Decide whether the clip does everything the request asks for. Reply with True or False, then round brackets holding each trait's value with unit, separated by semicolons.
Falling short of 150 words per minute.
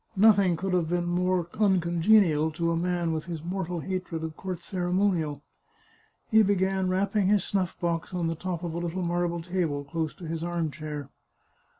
False (180 wpm)